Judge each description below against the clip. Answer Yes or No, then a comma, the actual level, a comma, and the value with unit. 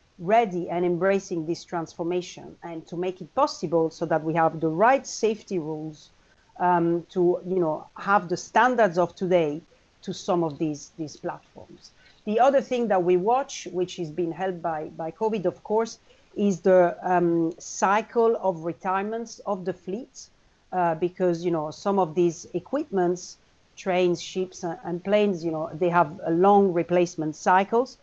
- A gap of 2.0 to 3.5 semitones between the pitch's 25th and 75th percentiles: Yes, average, 2.7 semitones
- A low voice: No, medium, 180 Hz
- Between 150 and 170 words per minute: Yes, average, 165 wpm